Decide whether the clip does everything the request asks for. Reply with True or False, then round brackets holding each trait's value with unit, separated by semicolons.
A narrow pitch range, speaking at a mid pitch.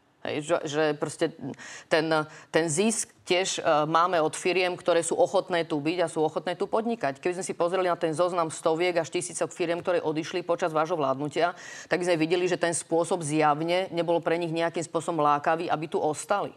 True (2.0 semitones; 170 Hz)